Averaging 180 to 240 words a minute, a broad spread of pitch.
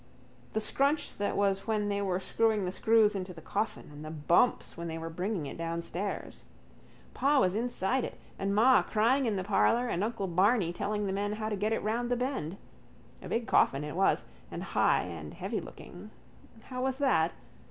No: average, 195 wpm; average, 4.1 semitones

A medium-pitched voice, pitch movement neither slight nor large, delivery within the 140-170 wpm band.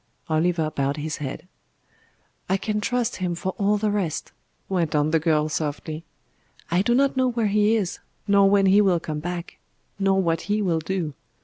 No: medium, 180 Hz; average, 4.5 semitones; average, 185 wpm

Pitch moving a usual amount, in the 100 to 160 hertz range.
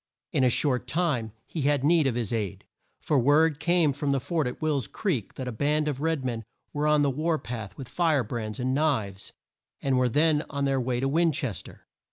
Yes: average, 3.6 semitones; medium, 140 Hz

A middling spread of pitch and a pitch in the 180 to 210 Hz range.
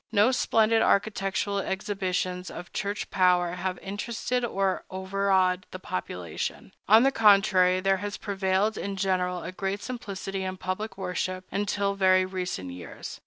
No: narrow, 1.7 semitones; high, 190 Hz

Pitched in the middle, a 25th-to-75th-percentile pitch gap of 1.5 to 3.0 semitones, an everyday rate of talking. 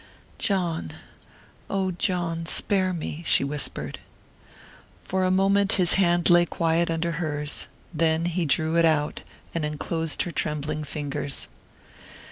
No: medium, 165 Hz; narrow, 2.6 semitones; slow, 120 wpm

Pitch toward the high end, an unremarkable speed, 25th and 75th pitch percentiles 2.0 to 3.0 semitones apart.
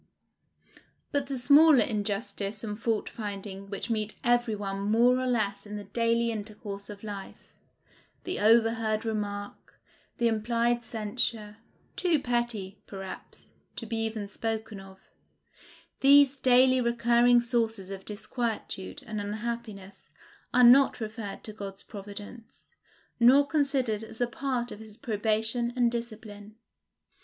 No: high, 225 Hz; slow, 130 wpm; narrow, 2.6 semitones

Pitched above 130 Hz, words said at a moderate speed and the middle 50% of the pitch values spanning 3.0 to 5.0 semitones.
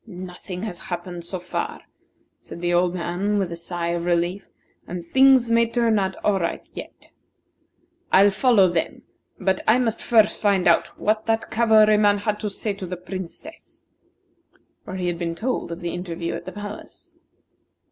Yes: high, 190 Hz; average, 170 wpm; average, 3.6 semitones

